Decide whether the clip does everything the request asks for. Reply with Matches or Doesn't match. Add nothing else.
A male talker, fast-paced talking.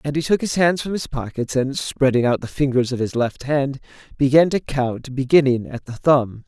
Matches